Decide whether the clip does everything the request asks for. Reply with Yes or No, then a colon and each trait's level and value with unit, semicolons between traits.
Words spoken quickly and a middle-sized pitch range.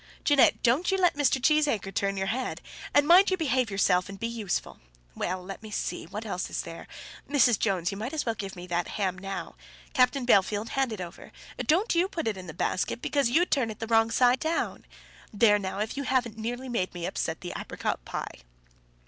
No: fast, 215 wpm; wide, 5.7 semitones